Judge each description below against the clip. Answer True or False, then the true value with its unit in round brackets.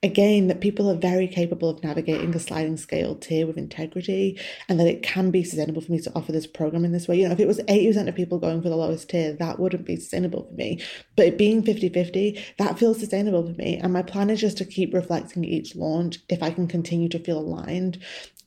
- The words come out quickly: True (240 wpm)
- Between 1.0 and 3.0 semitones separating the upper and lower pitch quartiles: True (2.7 semitones)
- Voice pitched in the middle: True (180 Hz)